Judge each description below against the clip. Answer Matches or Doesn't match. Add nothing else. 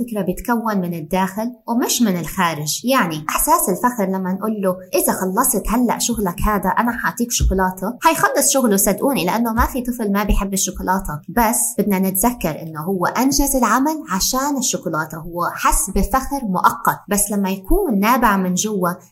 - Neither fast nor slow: Doesn't match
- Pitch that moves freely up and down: Doesn't match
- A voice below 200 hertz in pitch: Doesn't match